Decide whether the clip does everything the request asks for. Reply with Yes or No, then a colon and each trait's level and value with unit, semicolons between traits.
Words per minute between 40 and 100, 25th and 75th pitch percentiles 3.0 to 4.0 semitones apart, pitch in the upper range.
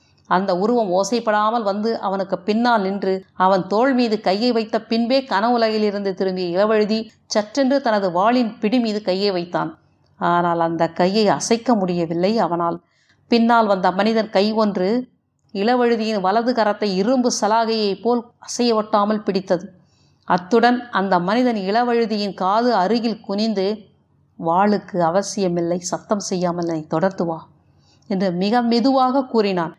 No: average, 115 wpm; average, 3.7 semitones; high, 205 Hz